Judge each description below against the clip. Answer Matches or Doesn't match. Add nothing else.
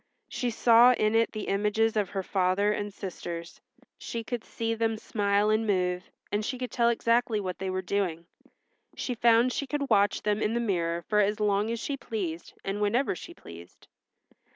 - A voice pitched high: Matches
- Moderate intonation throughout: Matches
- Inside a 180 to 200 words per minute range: Matches